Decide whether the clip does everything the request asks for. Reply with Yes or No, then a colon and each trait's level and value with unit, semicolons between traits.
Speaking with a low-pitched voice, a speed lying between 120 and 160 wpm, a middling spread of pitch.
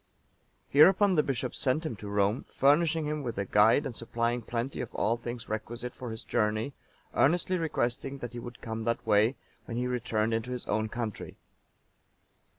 No: low, 120 Hz; average, 175 wpm; average, 3.6 semitones